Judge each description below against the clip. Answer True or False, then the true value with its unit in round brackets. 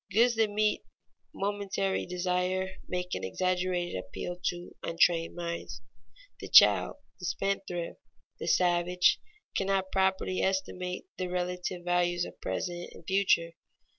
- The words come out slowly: True (120 wpm)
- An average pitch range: False (1.5 semitones)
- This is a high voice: False (180 Hz)